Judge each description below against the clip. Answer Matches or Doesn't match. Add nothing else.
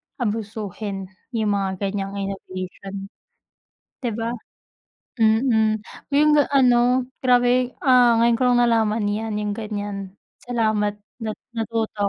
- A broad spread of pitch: Doesn't match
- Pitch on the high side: Matches